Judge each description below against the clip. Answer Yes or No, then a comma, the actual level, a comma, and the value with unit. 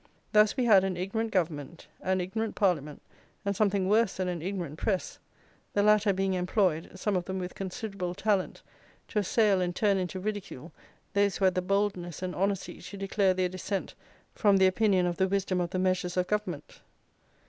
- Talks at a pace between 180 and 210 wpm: Yes, average, 185 wpm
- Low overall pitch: No, high, 190 Hz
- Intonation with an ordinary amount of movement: No, narrow, 2.1 semitones